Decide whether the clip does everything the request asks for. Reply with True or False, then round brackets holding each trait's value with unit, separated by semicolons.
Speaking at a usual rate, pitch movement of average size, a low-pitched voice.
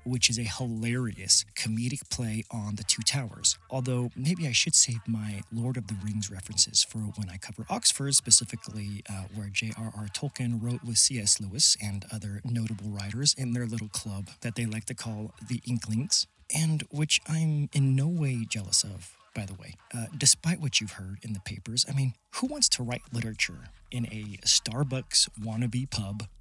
True (185 wpm; 3.1 semitones; 115 Hz)